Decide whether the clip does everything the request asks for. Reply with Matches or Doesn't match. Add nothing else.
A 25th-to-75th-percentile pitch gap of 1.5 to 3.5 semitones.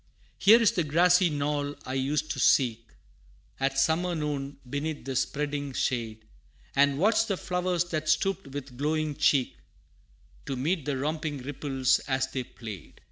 Matches